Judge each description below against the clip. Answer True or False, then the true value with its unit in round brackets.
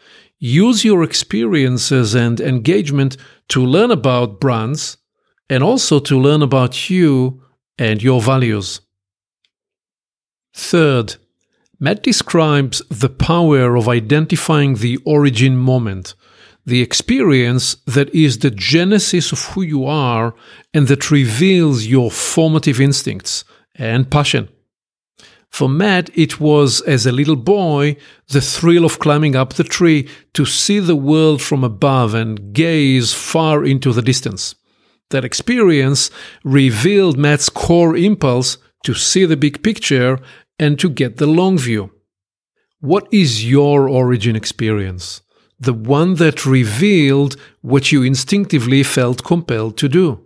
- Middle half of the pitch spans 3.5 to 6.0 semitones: True (4.0 semitones)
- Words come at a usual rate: False (125 wpm)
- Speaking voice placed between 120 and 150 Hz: True (140 Hz)